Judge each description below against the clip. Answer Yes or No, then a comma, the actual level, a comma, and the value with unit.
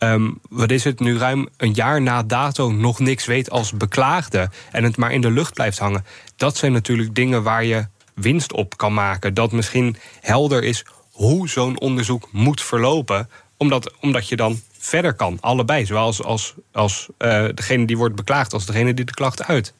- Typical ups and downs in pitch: Yes, average, 3.0 semitones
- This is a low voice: Yes, low, 120 Hz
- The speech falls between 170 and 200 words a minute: Yes, average, 195 wpm